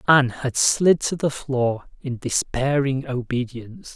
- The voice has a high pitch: No, low, 130 Hz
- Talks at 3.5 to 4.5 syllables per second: Yes, 4.2 syllables/s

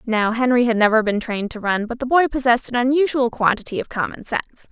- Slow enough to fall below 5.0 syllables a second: No, 6.3 syllables/s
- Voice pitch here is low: No, high, 240 Hz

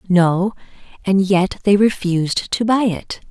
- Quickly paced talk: No, average, 145 wpm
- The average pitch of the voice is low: No, high, 190 Hz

